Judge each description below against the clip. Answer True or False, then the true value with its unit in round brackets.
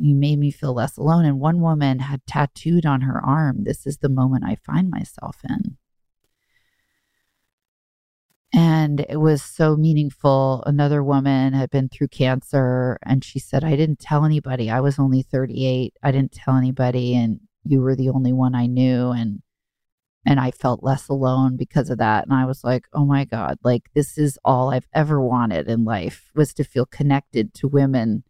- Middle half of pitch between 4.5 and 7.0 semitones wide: False (2.4 semitones)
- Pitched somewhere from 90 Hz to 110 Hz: False (135 Hz)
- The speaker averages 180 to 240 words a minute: True (185 wpm)